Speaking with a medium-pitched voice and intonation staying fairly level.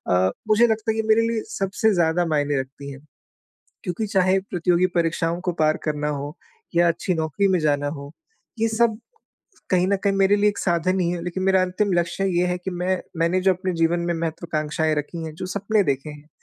No: medium, 175 Hz; average, 3.4 semitones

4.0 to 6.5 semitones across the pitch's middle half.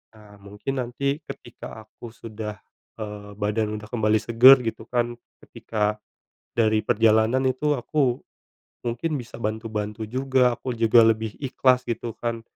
No: narrow, 2.6 semitones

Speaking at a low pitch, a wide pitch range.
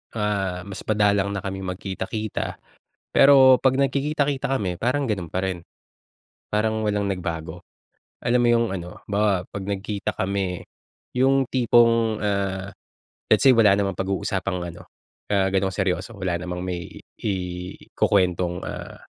No: low, 100 Hz; average, 3.7 semitones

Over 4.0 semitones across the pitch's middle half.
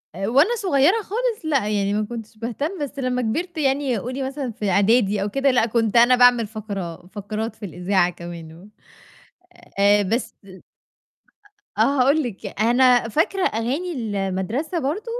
Yes: average, 5.3 semitones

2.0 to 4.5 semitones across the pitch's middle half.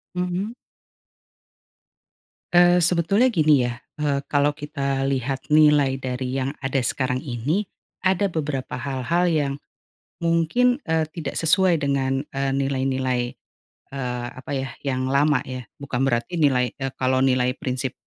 Yes: average, 3.7 semitones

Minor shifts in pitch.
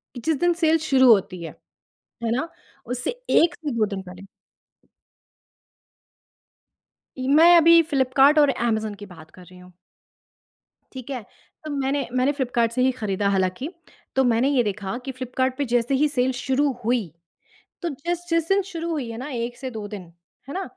No: average, 4.8 semitones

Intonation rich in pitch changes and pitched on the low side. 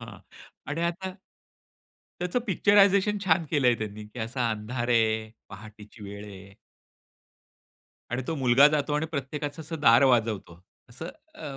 Yes: wide, 6.6 semitones; low, 125 Hz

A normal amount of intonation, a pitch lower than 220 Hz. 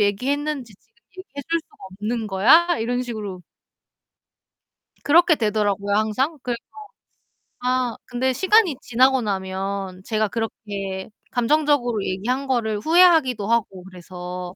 No: average, 5.0 semitones; high, 230 Hz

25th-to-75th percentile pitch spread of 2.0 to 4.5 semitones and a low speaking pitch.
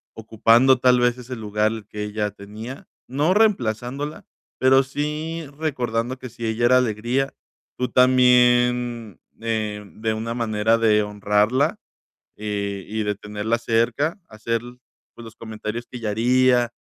Yes: average, 2.8 semitones; low, 115 Hz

